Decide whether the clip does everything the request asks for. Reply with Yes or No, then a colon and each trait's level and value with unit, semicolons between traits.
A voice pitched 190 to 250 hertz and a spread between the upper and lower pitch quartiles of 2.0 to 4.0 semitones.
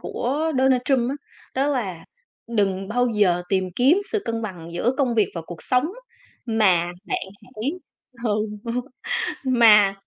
No: high, 225 Hz; average, 4.9 semitones